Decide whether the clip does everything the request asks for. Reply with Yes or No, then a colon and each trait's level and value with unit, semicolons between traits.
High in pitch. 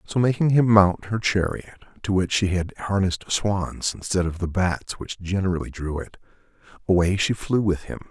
No: very low, 95 Hz